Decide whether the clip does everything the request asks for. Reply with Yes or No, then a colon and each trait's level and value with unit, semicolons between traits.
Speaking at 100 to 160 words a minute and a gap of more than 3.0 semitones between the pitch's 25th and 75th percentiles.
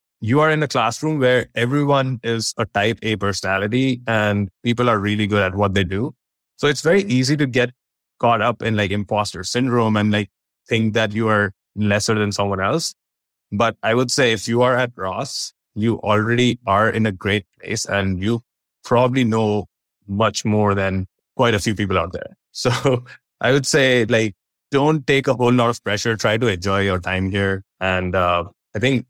No: average, 195 wpm; average, 3.5 semitones